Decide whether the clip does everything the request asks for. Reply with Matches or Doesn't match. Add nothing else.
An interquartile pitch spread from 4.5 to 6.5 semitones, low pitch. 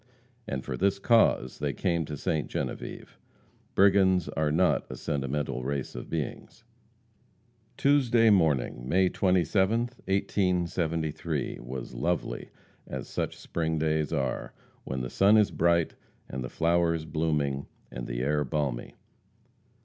Matches